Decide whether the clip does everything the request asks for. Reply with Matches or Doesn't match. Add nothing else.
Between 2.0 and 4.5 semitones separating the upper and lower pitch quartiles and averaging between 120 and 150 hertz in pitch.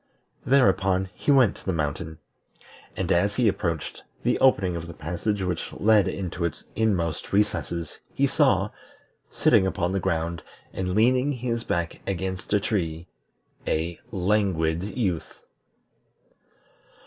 Doesn't match